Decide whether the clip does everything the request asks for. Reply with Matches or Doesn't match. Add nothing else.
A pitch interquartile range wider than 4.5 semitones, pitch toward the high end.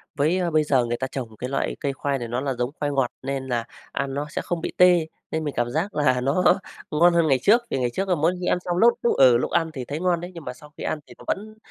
Doesn't match